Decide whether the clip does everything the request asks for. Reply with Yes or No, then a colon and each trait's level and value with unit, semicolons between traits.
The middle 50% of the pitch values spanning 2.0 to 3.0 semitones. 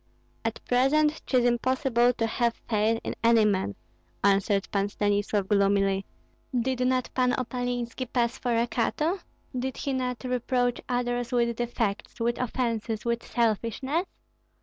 Yes: narrow, 2.4 semitones